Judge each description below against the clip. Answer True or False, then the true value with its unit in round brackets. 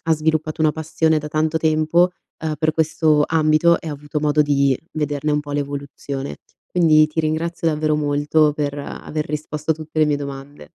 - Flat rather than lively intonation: True (1.4 semitones)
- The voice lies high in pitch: False (155 Hz)